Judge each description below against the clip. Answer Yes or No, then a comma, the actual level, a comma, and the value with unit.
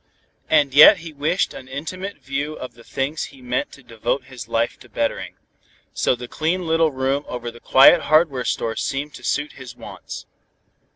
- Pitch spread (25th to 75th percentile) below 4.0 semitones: Yes, average, 3.5 semitones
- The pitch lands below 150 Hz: Yes, medium, 140 Hz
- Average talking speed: Yes, average, 180 wpm